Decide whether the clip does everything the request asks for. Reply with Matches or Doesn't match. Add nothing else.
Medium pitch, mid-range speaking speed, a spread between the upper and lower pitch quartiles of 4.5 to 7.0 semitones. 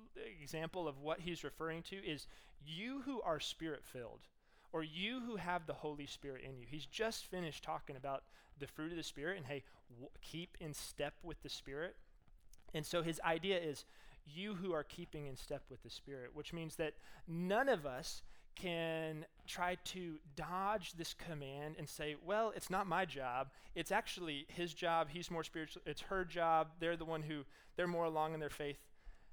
Doesn't match